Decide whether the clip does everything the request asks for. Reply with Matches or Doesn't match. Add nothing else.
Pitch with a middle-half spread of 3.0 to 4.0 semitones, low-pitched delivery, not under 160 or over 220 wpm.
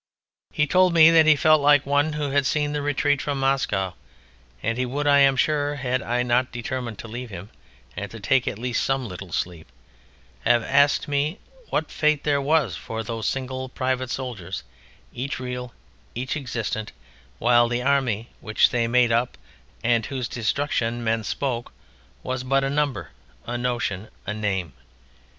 Matches